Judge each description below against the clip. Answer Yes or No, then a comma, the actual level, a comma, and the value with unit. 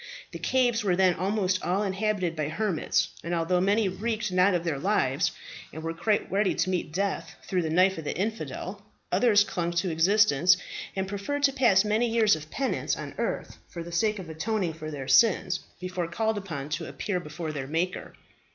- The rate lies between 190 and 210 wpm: Yes, average, 195 wpm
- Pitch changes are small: No, average, 4.0 semitones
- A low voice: No, medium, 185 Hz